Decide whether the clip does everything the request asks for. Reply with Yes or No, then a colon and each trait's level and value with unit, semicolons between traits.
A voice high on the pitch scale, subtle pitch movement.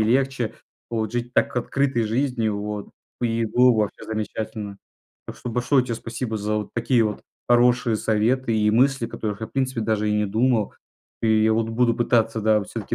No: low, 115 Hz; narrow, 2.3 semitones